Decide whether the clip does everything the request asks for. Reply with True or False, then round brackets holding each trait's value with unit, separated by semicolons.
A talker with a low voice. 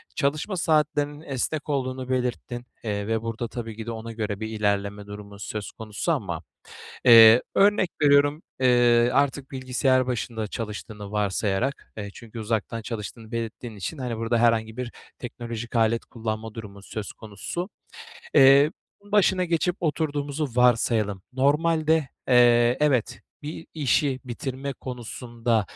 True (120 Hz)